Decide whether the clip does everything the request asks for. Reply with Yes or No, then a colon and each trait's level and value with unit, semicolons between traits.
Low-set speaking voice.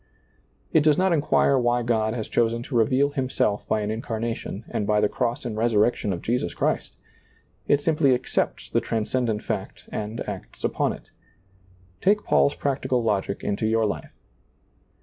Yes: low, 115 Hz